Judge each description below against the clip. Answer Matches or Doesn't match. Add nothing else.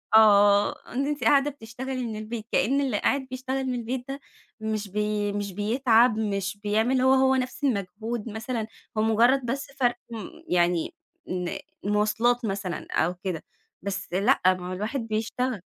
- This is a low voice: Doesn't match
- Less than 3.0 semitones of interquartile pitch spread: Doesn't match